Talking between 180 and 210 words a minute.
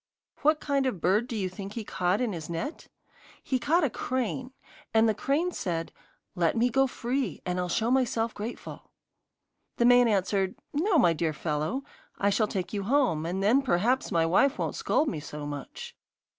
Yes: average, 185 wpm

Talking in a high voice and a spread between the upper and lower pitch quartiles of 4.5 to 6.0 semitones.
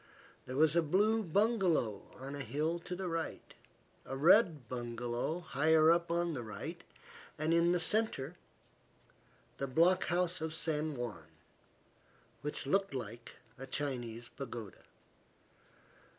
No: medium, 155 Hz; average, 5.3 semitones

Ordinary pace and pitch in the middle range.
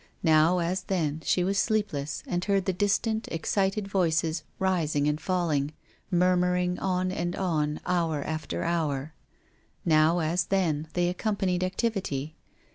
No: slow, 130 wpm; medium, 175 Hz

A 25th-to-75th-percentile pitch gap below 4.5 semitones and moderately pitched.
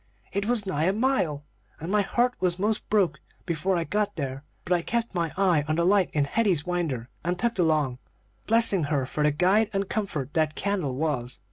No: average, 5.2 semitones; medium, 175 Hz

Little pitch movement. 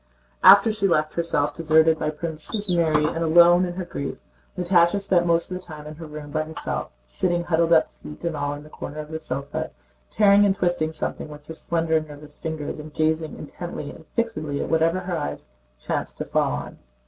Yes: narrow, 2.3 semitones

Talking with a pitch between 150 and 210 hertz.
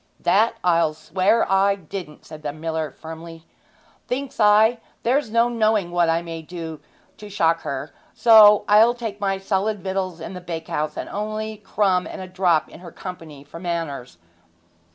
Yes: medium, 185 Hz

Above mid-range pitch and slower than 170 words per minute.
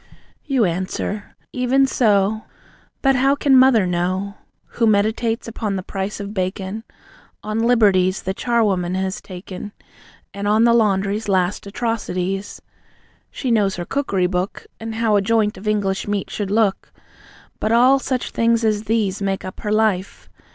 Yes: high, 210 Hz; average, 150 wpm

